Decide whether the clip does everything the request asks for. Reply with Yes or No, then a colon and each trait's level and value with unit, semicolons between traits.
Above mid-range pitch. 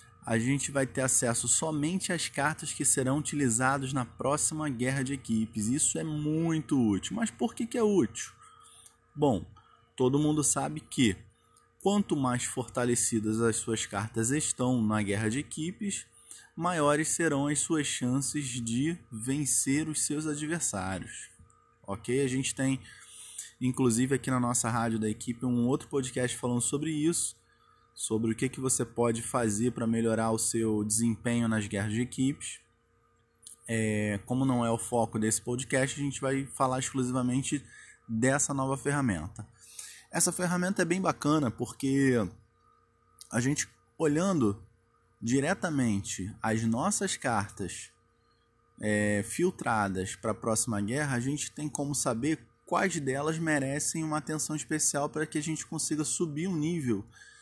No: low, 130 Hz